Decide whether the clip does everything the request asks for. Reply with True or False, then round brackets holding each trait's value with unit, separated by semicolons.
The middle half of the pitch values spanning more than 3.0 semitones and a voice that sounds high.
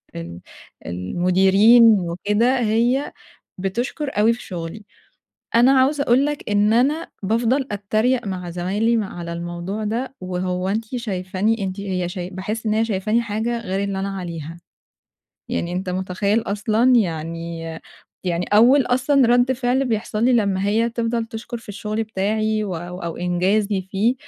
True (4.1 semitones; 210 Hz)